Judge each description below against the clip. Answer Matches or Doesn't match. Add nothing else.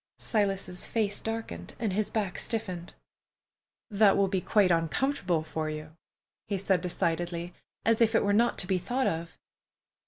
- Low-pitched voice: Doesn't match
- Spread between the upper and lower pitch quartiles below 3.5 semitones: Doesn't match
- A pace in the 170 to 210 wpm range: Doesn't match